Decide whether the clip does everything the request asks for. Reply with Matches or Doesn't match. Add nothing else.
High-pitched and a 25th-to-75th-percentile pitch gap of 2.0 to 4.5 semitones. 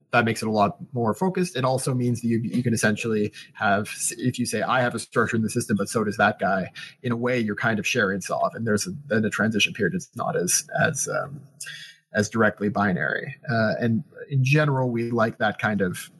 Doesn't match